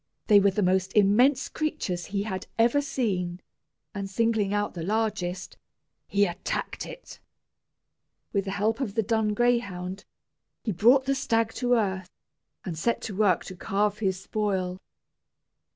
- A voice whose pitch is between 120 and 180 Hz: No, high, 205 Hz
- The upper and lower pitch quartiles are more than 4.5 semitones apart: No, average, 3.2 semitones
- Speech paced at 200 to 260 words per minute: No, average, 150 wpm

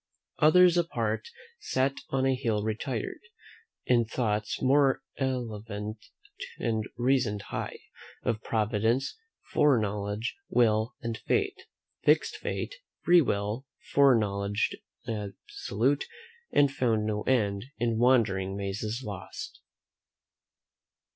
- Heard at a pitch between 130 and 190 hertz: No, low, 115 Hz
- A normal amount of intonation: Yes, average, 3.9 semitones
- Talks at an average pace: No, slow, 100 wpm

